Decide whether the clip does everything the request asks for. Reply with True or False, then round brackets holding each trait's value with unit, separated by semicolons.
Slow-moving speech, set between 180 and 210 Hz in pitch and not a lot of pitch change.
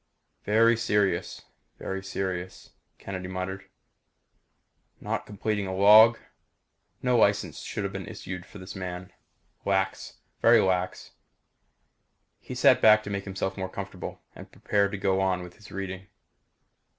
False (130 wpm; 95 Hz; 1.7 semitones)